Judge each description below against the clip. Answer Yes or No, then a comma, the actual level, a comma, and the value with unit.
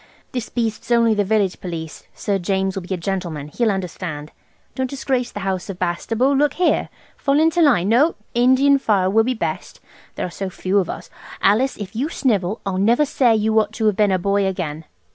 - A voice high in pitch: Yes, high, 210 Hz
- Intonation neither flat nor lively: Yes, average, 4.6 semitones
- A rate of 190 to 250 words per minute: Yes, average, 200 wpm